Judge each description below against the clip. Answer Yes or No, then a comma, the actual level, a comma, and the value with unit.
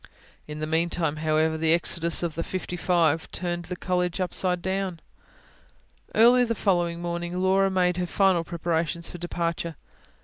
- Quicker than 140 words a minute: Yes, average, 150 wpm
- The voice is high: No, medium, 175 Hz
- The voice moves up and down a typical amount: No, narrow, 1.7 semitones